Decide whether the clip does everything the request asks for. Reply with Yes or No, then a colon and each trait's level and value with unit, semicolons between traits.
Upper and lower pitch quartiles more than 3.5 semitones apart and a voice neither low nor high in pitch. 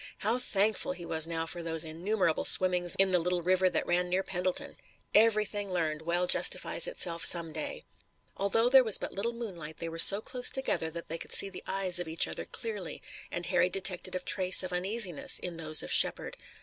No: average, 3.2 semitones; medium, 180 Hz